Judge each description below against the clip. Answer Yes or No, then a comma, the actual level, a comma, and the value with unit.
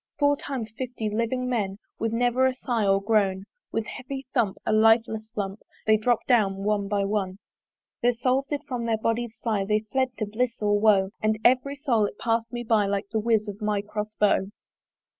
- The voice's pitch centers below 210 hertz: No, high, 220 Hz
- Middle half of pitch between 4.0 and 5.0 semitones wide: No, average, 2.9 semitones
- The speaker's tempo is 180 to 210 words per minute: Yes, average, 195 wpm